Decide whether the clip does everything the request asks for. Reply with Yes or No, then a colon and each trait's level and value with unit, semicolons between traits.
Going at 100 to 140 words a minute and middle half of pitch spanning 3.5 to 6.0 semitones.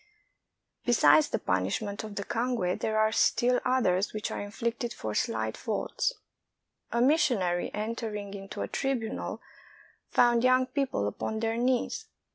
Yes: slow, 135 wpm; average, 3.8 semitones